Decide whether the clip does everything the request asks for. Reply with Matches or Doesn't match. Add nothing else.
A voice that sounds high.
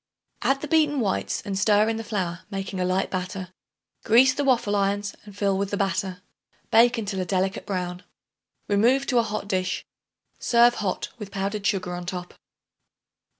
Matches